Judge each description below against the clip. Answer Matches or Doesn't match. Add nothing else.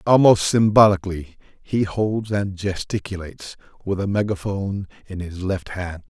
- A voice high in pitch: Doesn't match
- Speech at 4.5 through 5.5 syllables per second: Matches